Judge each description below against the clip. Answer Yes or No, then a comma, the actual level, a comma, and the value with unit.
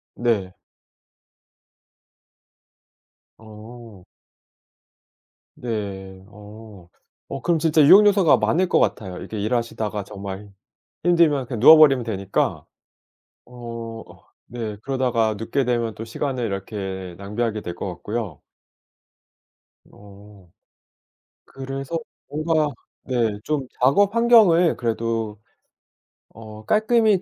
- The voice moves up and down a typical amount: Yes, average, 4.9 semitones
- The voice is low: Yes, low, 115 Hz